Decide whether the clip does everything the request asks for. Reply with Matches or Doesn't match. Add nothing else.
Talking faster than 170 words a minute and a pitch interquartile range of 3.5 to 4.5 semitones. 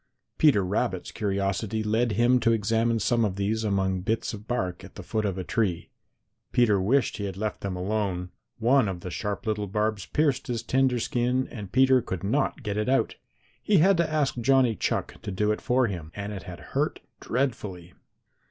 Matches